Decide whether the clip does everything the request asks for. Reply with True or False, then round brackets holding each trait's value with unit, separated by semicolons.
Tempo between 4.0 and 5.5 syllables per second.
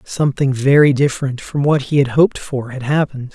False (5.9 syllables/s)